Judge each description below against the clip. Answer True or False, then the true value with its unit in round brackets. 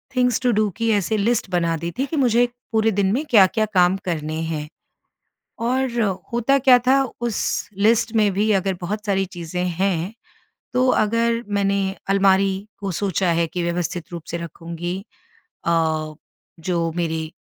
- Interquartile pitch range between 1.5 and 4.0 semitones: False (5.0 semitones)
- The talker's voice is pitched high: True (195 Hz)